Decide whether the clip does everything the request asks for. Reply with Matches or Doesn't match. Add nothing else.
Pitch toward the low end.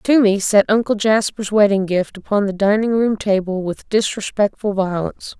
Doesn't match